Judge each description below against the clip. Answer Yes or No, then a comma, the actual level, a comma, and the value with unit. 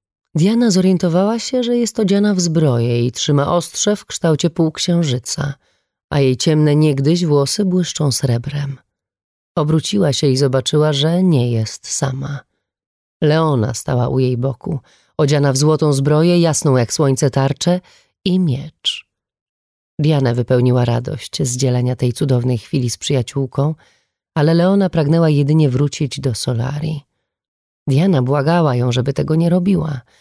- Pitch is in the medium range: Yes, medium, 145 Hz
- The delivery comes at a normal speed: Yes, average, 135 wpm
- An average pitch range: Yes, average, 4.1 semitones